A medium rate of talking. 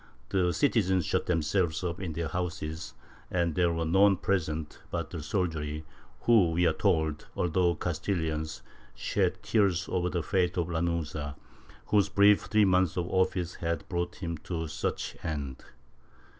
Yes: average, 150 wpm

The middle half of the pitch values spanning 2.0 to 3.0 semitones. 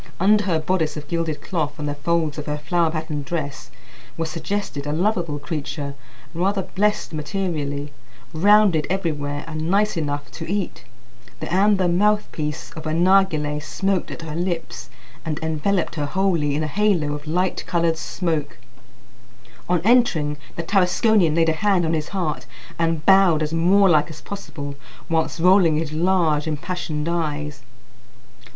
No: average, 3.7 semitones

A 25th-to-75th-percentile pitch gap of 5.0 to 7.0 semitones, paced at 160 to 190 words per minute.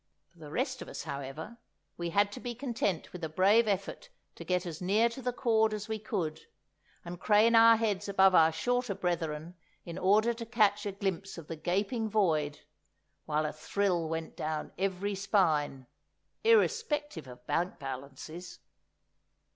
Yes: wide, 5.4 semitones; average, 165 wpm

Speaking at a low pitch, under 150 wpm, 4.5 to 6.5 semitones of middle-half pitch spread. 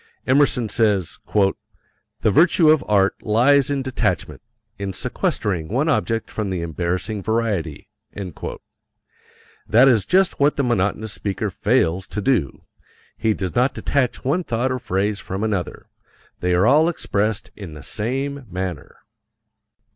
Yes: low, 110 Hz; slow, 135 wpm; wide, 5.4 semitones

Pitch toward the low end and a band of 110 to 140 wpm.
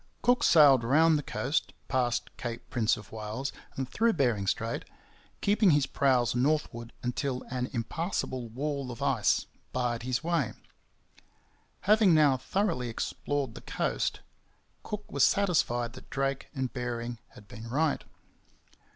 Yes: low, 130 Hz; slow, 135 wpm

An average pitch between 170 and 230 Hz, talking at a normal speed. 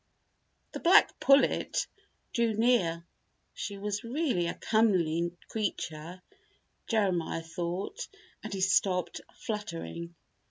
No: high, 190 Hz; slow, 95 wpm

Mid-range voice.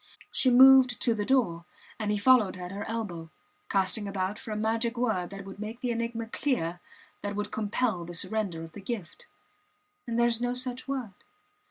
No: high, 220 Hz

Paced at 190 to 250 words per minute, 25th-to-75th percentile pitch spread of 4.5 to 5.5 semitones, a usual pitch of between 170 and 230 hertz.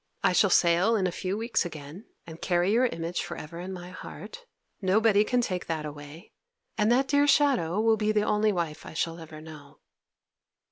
Yes: average, 195 wpm; average, 4.9 semitones; medium, 185 Hz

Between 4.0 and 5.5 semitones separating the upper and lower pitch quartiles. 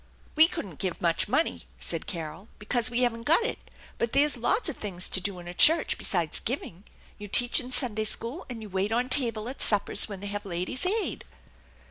Yes: average, 5.0 semitones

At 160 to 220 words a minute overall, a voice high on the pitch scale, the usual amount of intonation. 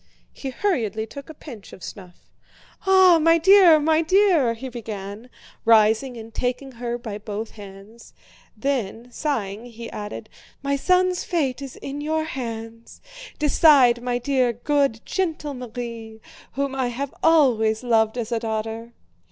No: average, 145 wpm; high, 245 Hz; average, 4.6 semitones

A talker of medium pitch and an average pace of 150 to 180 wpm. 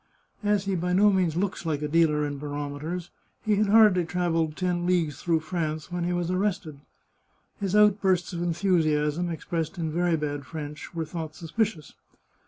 Yes: medium, 170 Hz; average, 175 wpm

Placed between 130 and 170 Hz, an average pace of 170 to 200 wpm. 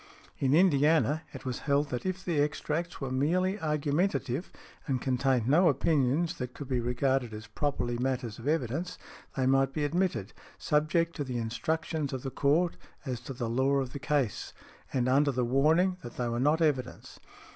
Yes: medium, 140 Hz; average, 180 wpm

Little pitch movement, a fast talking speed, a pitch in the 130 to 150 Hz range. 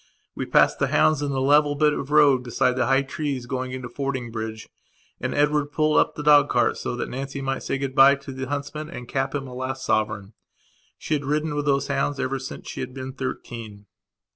Yes: narrow, 2.1 semitones; fast, 215 wpm; low, 135 Hz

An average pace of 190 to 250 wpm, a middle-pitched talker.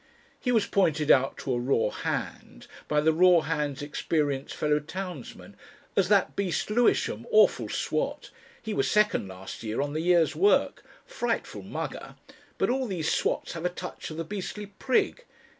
No: average, 165 wpm; medium, 165 Hz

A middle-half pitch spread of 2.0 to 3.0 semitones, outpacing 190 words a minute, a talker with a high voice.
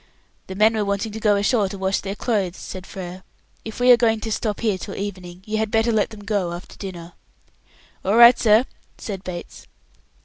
Yes: narrow, 2.6 semitones; average, 200 wpm; high, 205 Hz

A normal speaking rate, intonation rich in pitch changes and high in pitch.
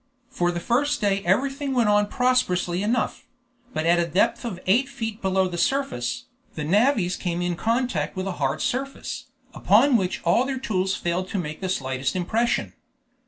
Yes: average, 175 wpm; wide, 5.8 semitones; high, 195 Hz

